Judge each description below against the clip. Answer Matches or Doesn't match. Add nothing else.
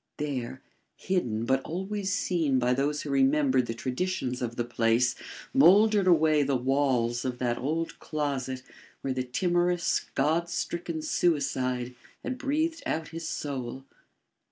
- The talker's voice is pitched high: Doesn't match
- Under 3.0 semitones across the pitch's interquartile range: Doesn't match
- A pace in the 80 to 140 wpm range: Matches